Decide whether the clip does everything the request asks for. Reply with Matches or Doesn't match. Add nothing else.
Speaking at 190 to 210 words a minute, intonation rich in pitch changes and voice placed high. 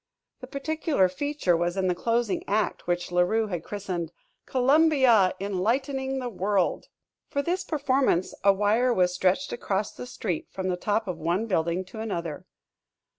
Doesn't match